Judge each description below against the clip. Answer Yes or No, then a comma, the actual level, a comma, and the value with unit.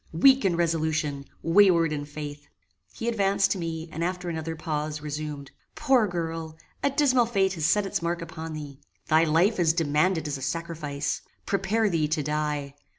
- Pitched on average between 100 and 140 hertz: No, medium, 165 Hz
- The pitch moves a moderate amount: Yes, average, 3.7 semitones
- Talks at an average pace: Yes, average, 170 wpm